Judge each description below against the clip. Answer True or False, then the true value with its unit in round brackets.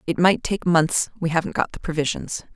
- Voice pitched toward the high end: False (170 Hz)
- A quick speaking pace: False (190 wpm)